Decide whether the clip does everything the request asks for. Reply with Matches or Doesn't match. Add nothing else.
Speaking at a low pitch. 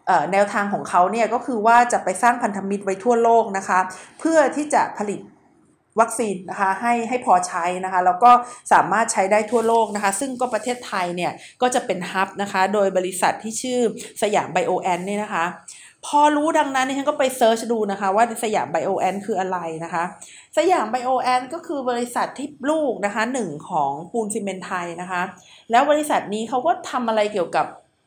Doesn't match